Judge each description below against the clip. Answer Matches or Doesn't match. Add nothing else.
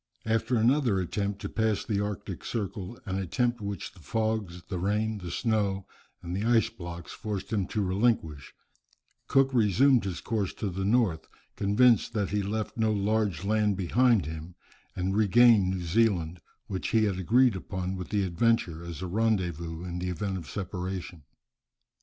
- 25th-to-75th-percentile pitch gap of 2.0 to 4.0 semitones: Matches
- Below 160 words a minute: Doesn't match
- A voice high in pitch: Doesn't match